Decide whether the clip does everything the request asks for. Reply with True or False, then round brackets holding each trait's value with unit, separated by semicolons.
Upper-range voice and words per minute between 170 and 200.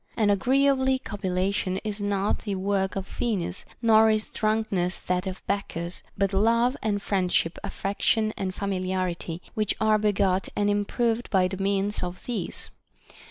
False (200 Hz; 145 wpm)